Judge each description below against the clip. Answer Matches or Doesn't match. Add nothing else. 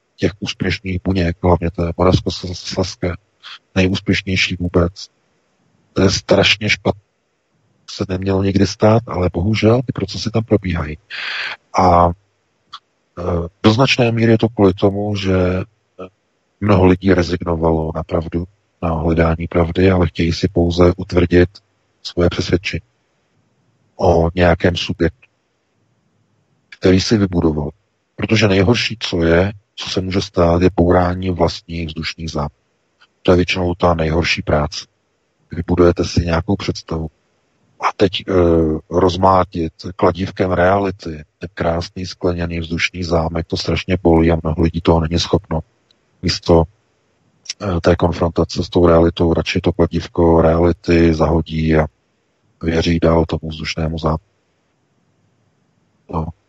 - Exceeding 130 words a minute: Doesn't match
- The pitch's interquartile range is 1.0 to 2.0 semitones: Doesn't match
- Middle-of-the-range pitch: Doesn't match